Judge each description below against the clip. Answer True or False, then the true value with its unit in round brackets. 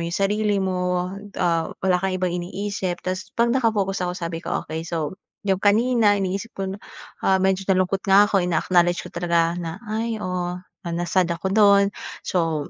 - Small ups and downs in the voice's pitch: True (2.3 semitones)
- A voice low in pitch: False (185 Hz)